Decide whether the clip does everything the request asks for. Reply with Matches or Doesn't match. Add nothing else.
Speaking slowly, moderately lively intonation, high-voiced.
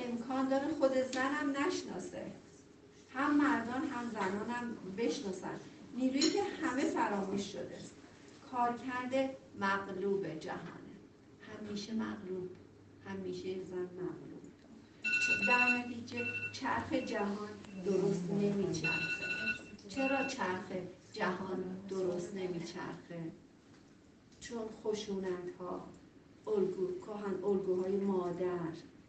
Doesn't match